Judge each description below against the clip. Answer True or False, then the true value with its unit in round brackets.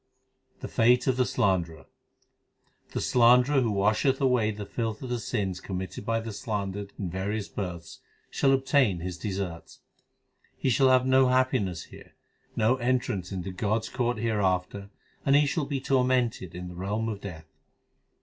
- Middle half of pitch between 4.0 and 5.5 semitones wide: True (5.1 semitones)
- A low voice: True (110 Hz)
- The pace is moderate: True (160 wpm)